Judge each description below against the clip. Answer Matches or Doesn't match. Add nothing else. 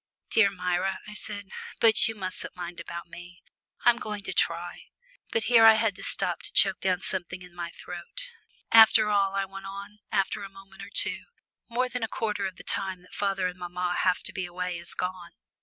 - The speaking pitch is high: Matches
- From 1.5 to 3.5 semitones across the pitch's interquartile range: Matches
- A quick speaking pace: Matches